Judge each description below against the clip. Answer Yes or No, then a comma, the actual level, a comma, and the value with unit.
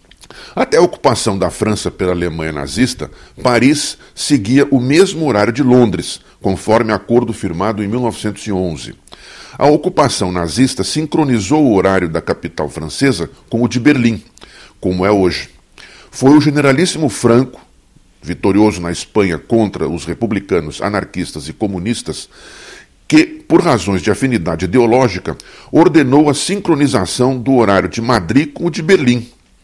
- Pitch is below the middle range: Yes, low, 115 Hz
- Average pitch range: No, wide, 6.4 semitones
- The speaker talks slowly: No, average, 135 wpm